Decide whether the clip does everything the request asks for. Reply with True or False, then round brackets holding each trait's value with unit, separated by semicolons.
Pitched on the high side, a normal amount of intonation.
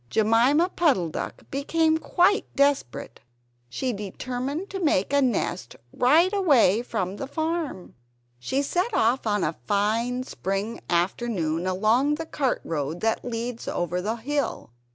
False (245 Hz; 6.9 semitones)